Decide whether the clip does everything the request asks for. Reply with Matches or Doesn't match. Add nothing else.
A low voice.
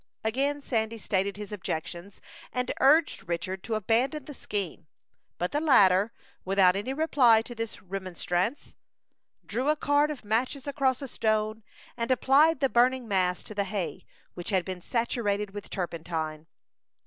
Doesn't match